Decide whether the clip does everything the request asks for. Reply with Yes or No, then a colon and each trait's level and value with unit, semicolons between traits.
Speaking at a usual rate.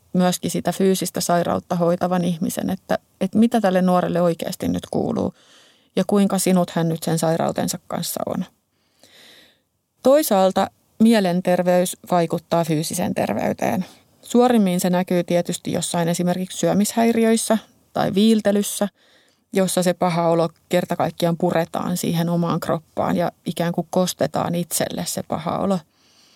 Yes: average, 125 wpm